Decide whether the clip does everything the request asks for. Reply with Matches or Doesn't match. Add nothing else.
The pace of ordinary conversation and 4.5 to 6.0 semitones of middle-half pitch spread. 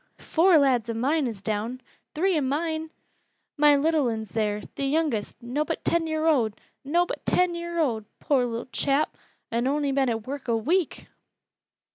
Matches